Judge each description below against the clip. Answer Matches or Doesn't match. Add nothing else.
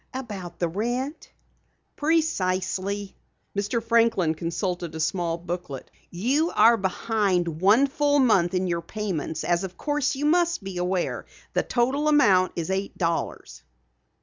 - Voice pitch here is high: Matches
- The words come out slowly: Matches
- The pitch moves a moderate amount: Doesn't match